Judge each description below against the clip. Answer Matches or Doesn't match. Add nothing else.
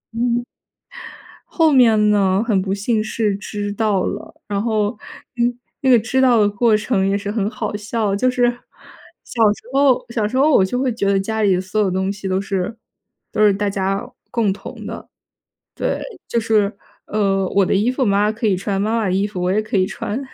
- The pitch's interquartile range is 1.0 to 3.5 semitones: Matches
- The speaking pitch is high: Matches